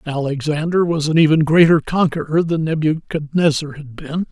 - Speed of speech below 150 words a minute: Yes, average, 140 wpm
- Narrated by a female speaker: No, male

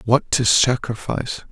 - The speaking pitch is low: Yes, low, 125 Hz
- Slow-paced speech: Yes, slow, 120 wpm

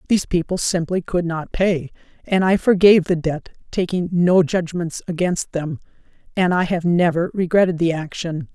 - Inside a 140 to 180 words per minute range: Yes, average, 160 wpm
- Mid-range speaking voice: Yes, medium, 175 Hz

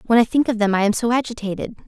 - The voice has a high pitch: Yes, high, 225 Hz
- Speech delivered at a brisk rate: Yes, fast, 290 wpm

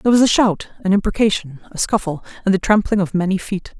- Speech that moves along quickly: Yes, fast, 220 wpm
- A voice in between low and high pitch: No, high, 195 Hz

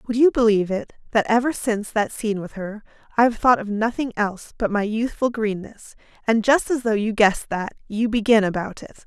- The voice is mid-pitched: No, high, 220 Hz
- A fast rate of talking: Yes, fast, 210 wpm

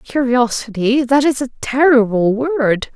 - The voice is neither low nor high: No, very high, 250 Hz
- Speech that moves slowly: Yes, slow, 100 wpm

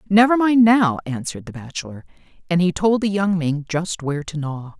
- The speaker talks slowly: No, average, 200 wpm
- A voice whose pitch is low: No, medium, 175 Hz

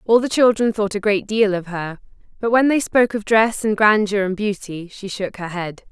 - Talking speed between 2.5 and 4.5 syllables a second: No, 5.1 syllables/s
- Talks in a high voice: Yes, high, 205 Hz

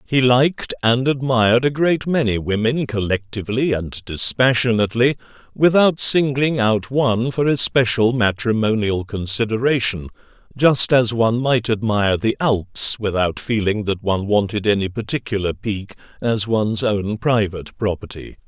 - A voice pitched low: Yes, low, 115 Hz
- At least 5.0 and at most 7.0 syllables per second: No, 4.8 syllables/s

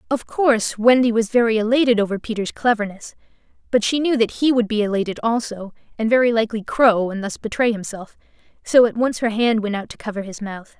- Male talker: No, female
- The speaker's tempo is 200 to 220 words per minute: Yes, fast, 205 wpm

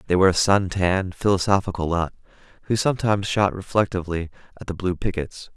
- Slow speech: No, average, 160 wpm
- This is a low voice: Yes, very low, 95 Hz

